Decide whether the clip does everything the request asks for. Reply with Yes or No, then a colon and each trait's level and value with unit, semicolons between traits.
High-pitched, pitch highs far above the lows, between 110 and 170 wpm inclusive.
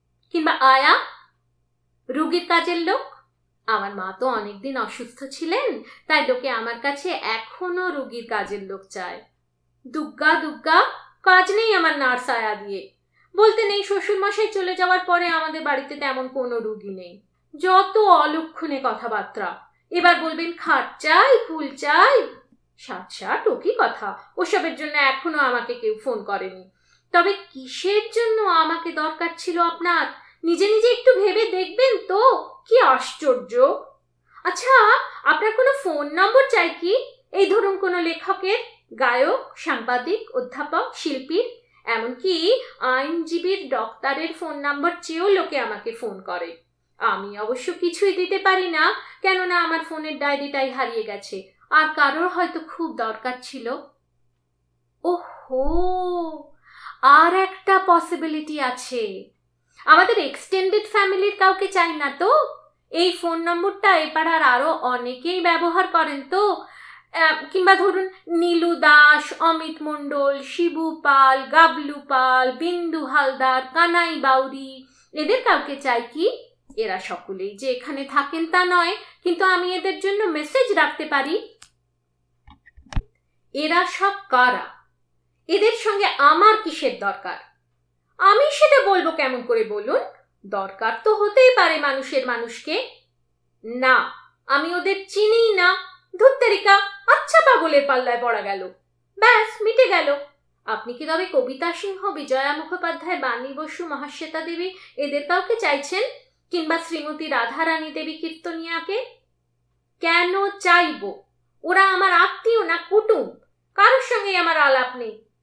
Yes: very high, 330 Hz; wide, 6.3 semitones; average, 115 wpm